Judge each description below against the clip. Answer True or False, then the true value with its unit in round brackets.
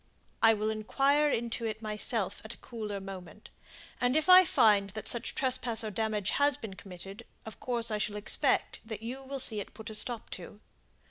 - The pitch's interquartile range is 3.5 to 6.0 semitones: False (3.0 semitones)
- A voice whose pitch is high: True (220 Hz)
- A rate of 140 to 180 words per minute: False (195 wpm)